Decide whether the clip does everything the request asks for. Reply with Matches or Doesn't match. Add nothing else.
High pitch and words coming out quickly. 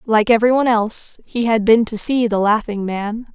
Matches